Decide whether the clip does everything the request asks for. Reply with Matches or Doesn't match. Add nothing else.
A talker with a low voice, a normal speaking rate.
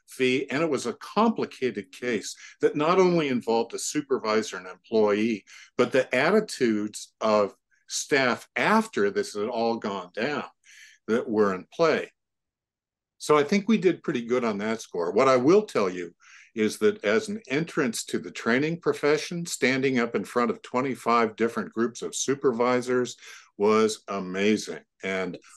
Matches